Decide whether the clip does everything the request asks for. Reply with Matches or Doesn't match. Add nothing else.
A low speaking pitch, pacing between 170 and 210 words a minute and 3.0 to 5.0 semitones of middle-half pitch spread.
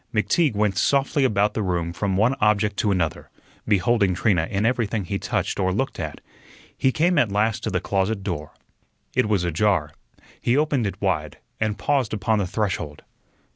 Matches